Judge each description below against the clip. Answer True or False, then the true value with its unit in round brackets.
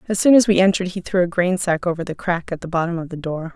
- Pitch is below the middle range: False (180 Hz)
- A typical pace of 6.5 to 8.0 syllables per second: True (6.9 syllables/s)